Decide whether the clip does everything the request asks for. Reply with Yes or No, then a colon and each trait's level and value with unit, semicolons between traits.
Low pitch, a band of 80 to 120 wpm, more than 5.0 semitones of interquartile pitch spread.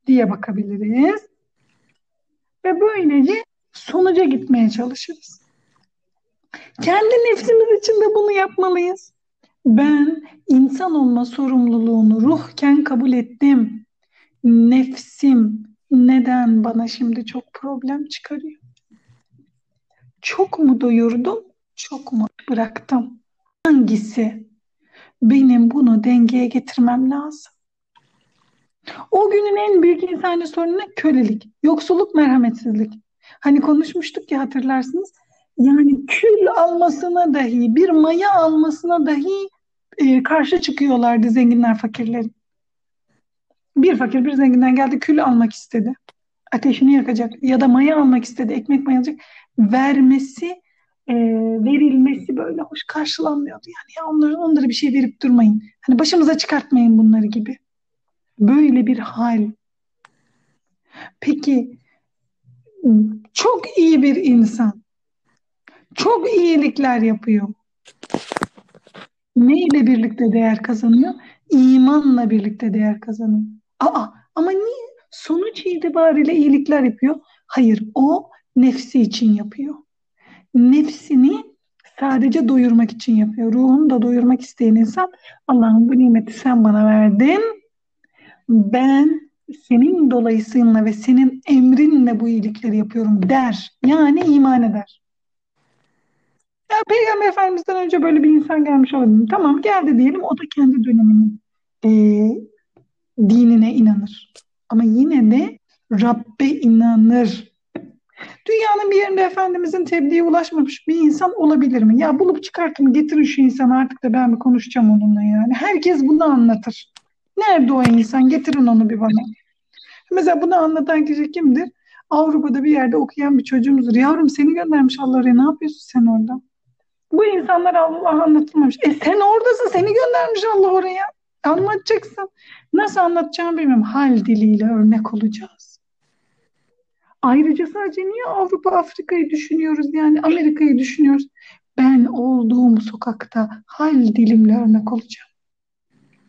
No: very high, 270 Hz; average, 115 wpm; wide, 5.5 semitones